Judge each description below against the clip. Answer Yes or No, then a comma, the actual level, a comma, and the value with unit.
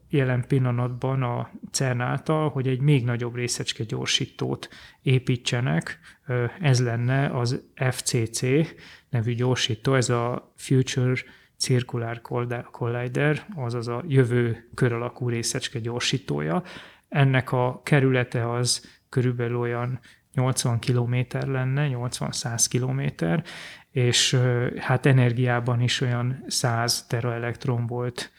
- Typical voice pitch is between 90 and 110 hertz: No, low, 125 Hz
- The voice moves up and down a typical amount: No, narrow, 1.5 semitones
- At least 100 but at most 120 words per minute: Yes, slow, 105 wpm